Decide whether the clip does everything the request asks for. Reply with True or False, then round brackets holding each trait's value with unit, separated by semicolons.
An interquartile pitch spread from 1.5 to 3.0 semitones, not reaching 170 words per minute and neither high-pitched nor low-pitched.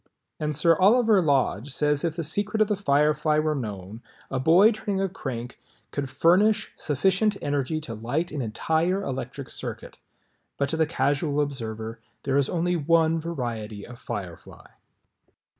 False (4.9 semitones; 155 wpm; 150 Hz)